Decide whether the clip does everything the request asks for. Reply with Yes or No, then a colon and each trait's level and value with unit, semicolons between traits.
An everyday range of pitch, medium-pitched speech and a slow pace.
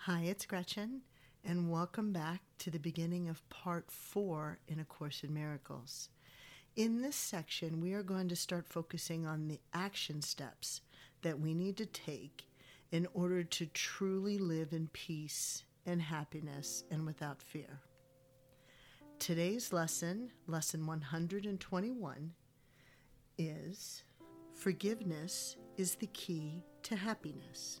Yes: average, 4.3 semitones; medium, 165 Hz; slow, 125 wpm